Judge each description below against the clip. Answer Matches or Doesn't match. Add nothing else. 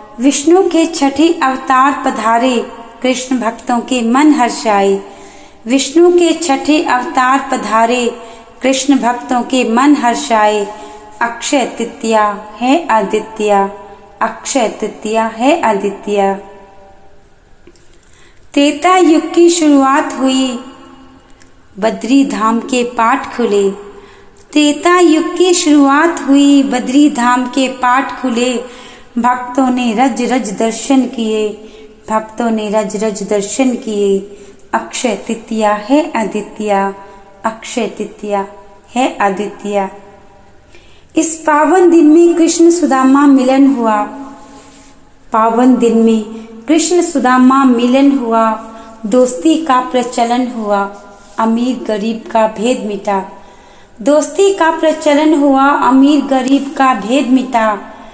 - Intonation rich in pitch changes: Doesn't match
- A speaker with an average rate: Doesn't match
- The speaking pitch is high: Matches